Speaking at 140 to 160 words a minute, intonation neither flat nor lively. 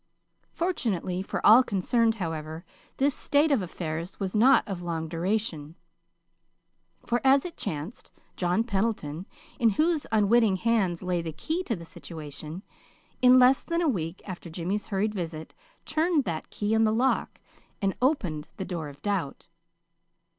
No: average, 150 wpm; wide, 6.1 semitones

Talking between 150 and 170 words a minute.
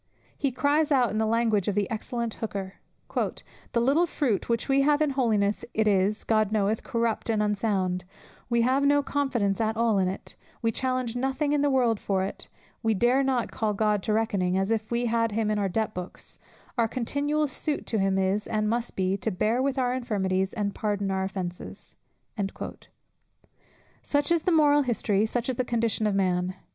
No: average, 190 wpm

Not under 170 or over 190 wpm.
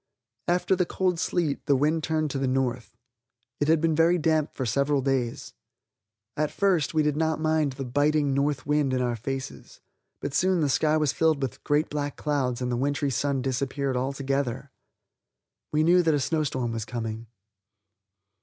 Yes: average, 175 wpm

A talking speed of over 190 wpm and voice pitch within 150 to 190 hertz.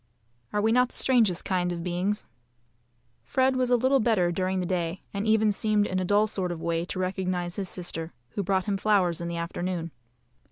Yes: fast, 205 wpm; medium, 185 Hz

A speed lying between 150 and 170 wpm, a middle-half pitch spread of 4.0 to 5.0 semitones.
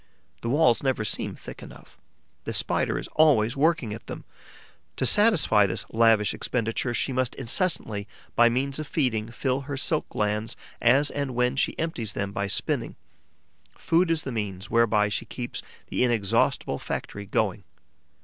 Yes: average, 160 wpm; average, 4.5 semitones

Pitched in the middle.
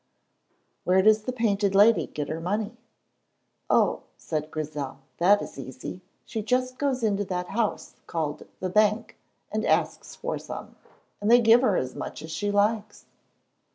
No: high, 205 Hz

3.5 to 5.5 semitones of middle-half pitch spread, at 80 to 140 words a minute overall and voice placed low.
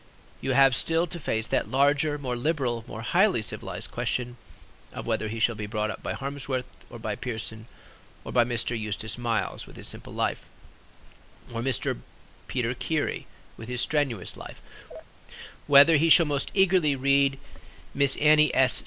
No: average, 4.0 semitones; average, 160 wpm; low, 130 Hz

